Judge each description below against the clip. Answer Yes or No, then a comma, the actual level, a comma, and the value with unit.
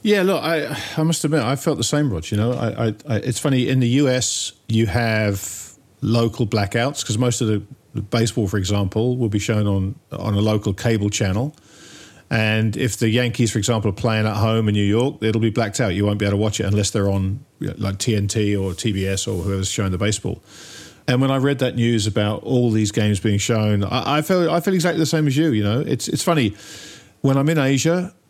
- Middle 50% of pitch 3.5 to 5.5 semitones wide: Yes, average, 4.5 semitones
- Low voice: Yes, low, 115 Hz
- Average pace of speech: No, fast, 235 wpm